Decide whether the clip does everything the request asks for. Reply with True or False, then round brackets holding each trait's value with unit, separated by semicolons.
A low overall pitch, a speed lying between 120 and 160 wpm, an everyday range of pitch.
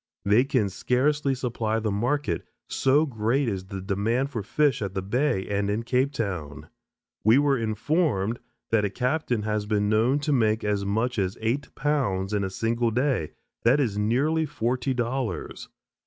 False (115 Hz; 170 wpm; 4.5 semitones)